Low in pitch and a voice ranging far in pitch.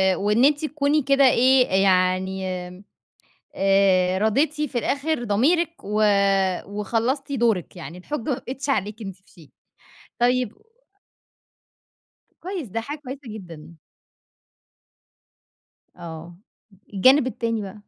No: high, 230 Hz; wide, 6.4 semitones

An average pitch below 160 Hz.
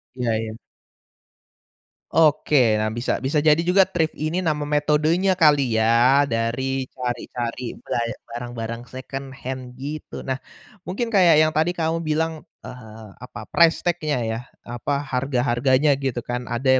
Yes: low, 135 Hz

